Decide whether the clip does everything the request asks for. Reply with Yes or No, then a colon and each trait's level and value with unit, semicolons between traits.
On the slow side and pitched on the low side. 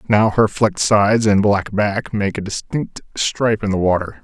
No: average, 200 wpm; low, 105 Hz